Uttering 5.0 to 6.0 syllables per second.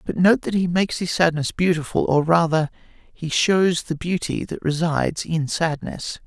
No: 4.6 syllables/s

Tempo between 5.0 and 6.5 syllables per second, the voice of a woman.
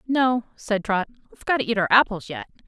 Yes: 6.1 syllables/s; female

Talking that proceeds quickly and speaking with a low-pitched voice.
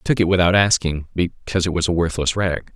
Yes: fast, 240 wpm; very low, 90 Hz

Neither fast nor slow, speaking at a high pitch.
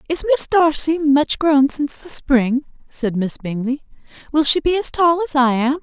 Yes: average, 195 wpm; very high, 285 Hz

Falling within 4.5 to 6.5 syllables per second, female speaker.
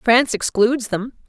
Yes: 5.1 syllables/s; female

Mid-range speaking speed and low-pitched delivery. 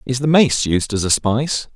No: fast, 240 wpm; low, 125 Hz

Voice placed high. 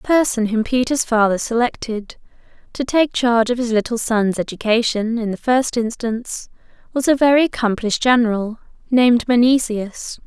Yes: high, 235 Hz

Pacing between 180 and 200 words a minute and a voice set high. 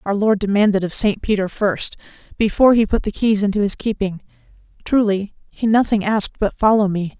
Yes: average, 185 wpm; high, 205 Hz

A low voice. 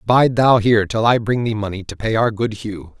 Yes: low, 110 Hz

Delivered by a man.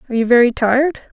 No: female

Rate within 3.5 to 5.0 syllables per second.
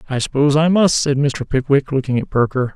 No: 5.9 syllables/s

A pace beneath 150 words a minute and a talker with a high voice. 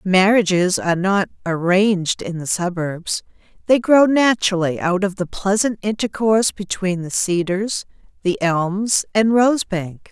Yes: slow, 135 wpm; high, 195 Hz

